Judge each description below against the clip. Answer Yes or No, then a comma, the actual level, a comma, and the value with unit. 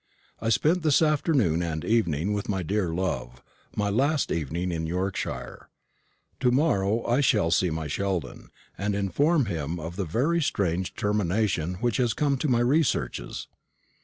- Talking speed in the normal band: Yes, average, 155 wpm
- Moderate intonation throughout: No, wide, 6.6 semitones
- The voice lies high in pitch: No, low, 100 Hz